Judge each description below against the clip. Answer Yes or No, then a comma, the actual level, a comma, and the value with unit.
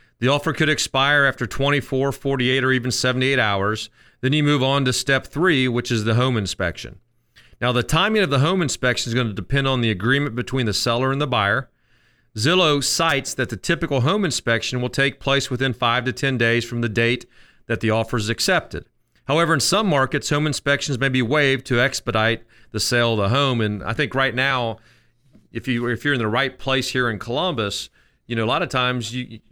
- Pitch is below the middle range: Yes, low, 125 Hz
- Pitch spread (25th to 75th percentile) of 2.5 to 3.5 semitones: Yes, average, 2.9 semitones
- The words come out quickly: Yes, fast, 215 wpm